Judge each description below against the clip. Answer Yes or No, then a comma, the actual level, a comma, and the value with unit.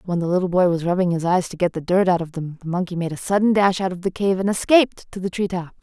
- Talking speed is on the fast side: Yes, fast, 320 wpm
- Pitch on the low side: No, medium, 180 Hz